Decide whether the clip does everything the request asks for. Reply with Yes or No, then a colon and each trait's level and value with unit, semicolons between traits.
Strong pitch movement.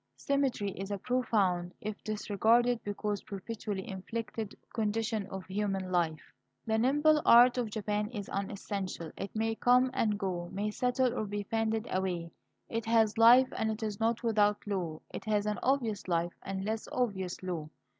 No: average, 2.8 semitones